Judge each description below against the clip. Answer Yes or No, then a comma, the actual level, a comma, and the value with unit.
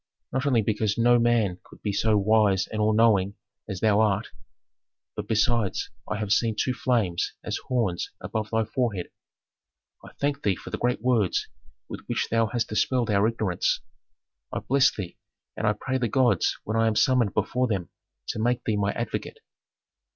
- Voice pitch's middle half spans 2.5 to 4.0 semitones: Yes, average, 2.8 semitones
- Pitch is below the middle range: Yes, low, 110 Hz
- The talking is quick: No, average, 180 wpm